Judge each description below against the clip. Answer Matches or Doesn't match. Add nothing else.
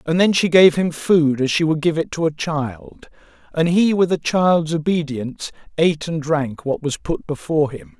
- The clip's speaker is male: Matches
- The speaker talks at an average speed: Doesn't match